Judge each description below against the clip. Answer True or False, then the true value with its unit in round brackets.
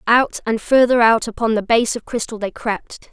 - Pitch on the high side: True (225 Hz)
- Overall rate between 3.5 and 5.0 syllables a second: True (4.8 syllables/s)